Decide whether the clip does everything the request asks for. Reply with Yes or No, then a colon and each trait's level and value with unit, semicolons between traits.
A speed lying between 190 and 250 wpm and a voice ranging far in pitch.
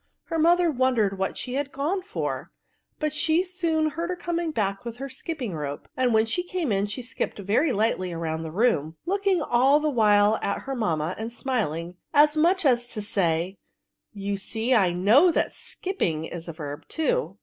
Yes: average, 195 wpm; wide, 8.2 semitones